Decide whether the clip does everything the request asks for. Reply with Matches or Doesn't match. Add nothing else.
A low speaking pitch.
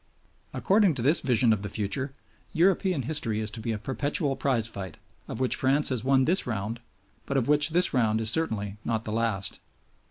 Matches